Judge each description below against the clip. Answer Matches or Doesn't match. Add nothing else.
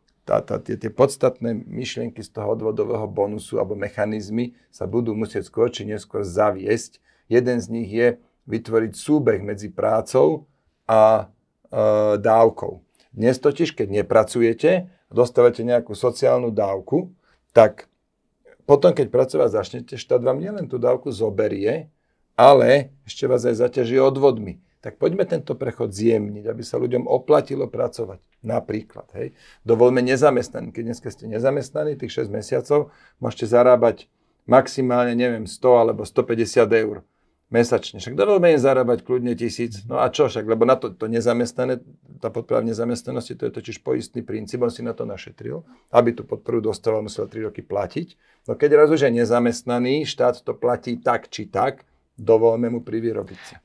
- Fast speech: Doesn't match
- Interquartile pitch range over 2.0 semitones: Matches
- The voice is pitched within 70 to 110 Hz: Doesn't match